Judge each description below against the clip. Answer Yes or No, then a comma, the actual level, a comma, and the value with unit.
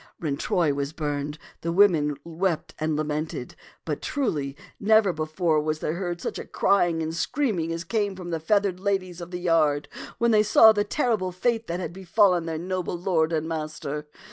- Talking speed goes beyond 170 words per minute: Yes, average, 185 wpm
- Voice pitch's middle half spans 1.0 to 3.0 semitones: No, average, 3.8 semitones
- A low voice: No, medium, 170 Hz